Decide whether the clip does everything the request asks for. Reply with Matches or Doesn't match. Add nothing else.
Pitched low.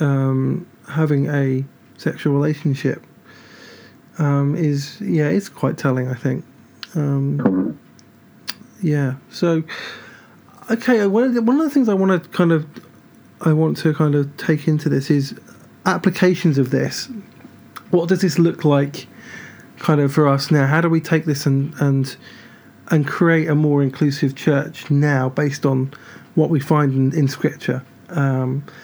Doesn't match